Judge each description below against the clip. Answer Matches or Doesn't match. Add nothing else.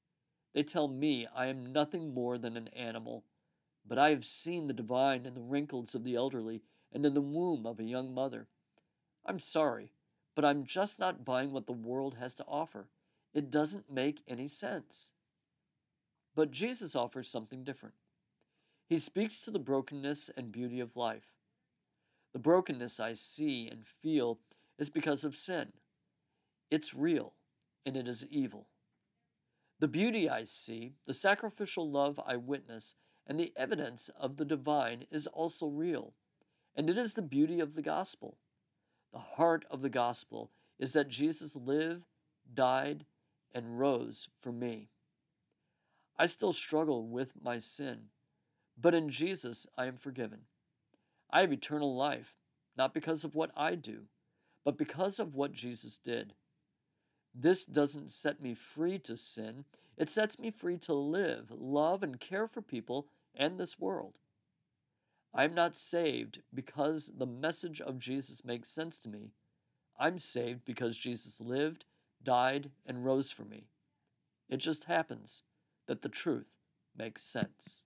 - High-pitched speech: Doesn't match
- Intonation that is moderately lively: Matches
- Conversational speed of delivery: Matches